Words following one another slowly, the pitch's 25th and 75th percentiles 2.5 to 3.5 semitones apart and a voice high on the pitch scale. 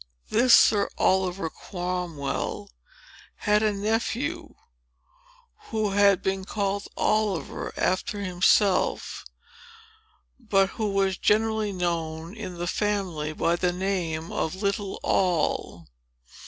Yes: slow, 100 wpm; average, 2.8 semitones; high, 195 Hz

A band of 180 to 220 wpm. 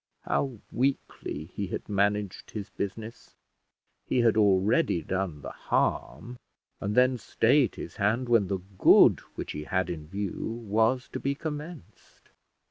No: average, 140 wpm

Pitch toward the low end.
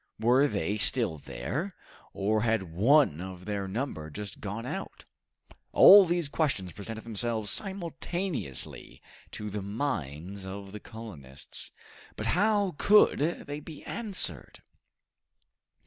Yes: low, 110 Hz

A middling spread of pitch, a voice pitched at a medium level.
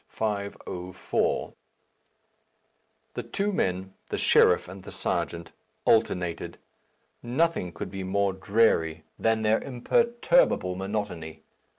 No: average, 3.8 semitones; low, 100 Hz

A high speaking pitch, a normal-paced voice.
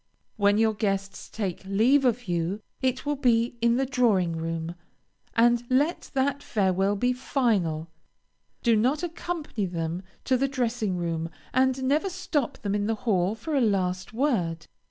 Yes: high, 225 Hz; average, 155 wpm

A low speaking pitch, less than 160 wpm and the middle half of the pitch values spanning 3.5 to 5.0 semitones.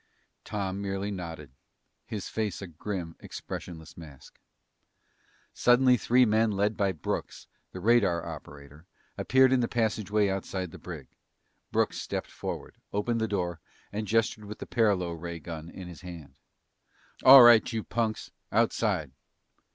Yes: low, 100 Hz; average, 140 wpm; average, 4.5 semitones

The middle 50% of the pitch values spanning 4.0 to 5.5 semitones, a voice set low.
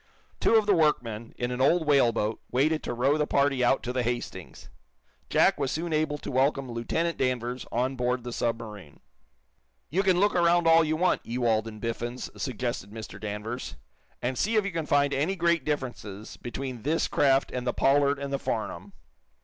Yes: average, 4.5 semitones; low, 130 Hz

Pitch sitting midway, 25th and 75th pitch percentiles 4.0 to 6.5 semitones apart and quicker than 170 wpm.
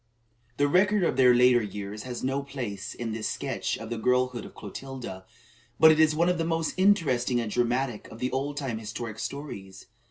No: low, 125 Hz; average, 4.3 semitones; average, 195 wpm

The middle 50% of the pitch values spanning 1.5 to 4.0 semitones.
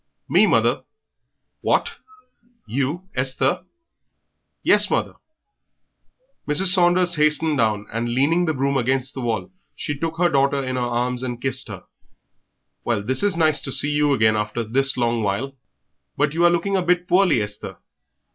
No: average, 5.3 semitones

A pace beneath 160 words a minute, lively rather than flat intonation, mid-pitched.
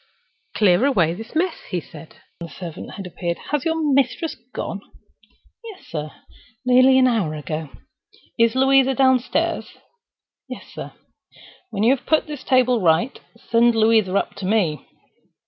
No: average, 140 wpm; wide, 6.9 semitones; high, 230 Hz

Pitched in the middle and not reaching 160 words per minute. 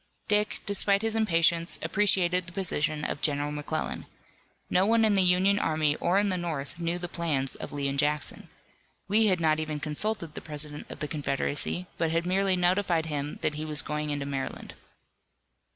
No: medium, 165 Hz; average, 185 wpm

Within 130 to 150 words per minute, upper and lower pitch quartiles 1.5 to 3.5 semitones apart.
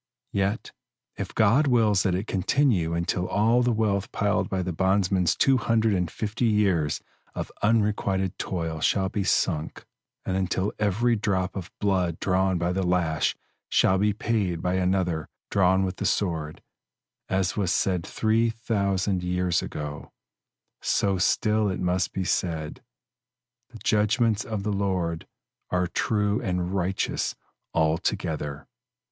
Yes: average, 140 wpm; average, 2.8 semitones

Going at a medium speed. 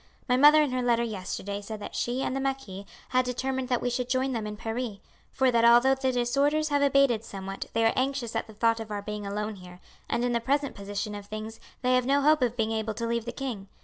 No: fast, 250 wpm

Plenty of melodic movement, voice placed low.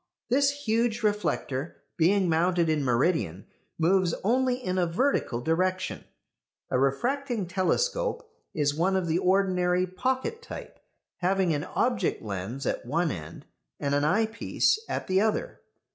No: wide, 5.9 semitones; medium, 185 Hz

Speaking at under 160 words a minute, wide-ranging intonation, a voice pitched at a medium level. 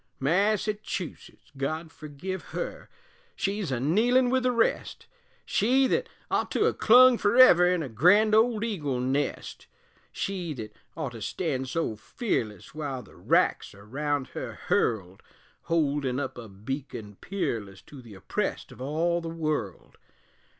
Yes: average, 145 wpm; wide, 7.9 semitones; medium, 155 Hz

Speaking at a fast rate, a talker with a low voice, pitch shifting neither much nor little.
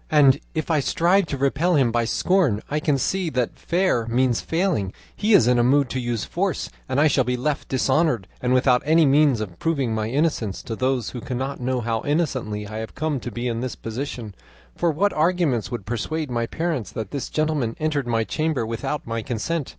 Yes: fast, 210 wpm; low, 130 Hz; average, 4.9 semitones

